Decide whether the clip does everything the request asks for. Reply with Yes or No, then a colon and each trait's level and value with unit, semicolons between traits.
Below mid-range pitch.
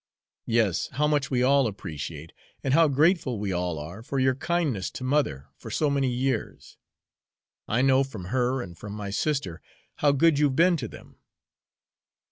Yes: low, 130 Hz